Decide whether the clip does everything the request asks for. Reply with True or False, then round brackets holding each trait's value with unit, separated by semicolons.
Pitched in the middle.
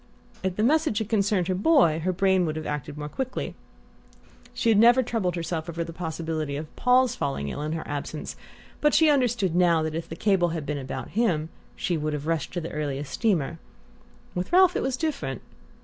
True (175 Hz)